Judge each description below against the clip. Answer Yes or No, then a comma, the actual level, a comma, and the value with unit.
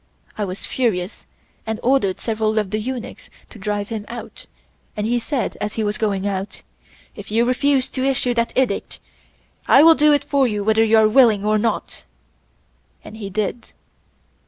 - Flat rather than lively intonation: No, average, 3.1 semitones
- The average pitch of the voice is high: Yes, high, 220 Hz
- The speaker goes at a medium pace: Yes, average, 180 wpm